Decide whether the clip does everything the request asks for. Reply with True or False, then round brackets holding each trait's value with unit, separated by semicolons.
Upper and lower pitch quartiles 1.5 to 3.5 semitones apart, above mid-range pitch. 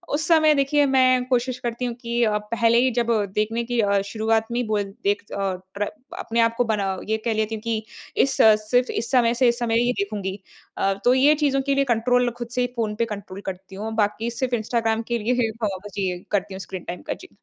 True (2.9 semitones; 230 Hz)